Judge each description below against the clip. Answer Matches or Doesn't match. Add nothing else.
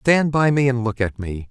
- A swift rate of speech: Matches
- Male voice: Matches